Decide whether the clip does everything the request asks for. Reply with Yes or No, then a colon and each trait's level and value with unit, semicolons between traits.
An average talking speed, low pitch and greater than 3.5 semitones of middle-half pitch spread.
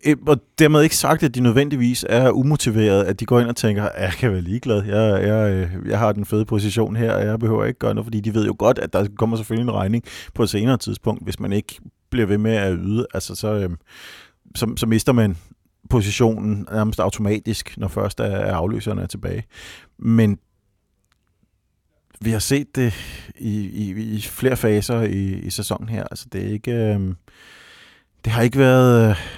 No: average, 190 wpm; low, 110 Hz; average, 2.7 semitones